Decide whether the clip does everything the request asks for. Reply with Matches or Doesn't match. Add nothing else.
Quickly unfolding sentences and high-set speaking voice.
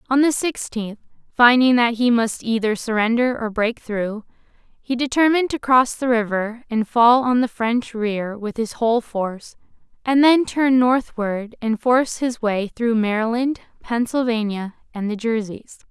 Doesn't match